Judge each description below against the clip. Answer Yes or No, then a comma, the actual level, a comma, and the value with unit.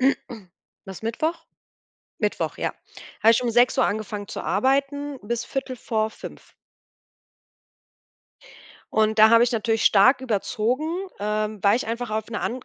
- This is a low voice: No, high, 230 Hz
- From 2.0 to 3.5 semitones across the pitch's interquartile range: Yes, average, 3.2 semitones